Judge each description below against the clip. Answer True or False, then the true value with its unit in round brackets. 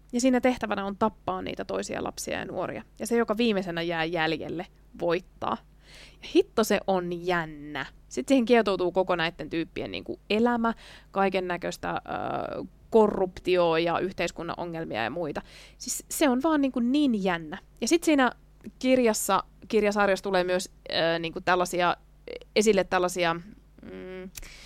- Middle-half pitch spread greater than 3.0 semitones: True (5.2 semitones)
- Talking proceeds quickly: False (140 wpm)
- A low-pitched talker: False (190 Hz)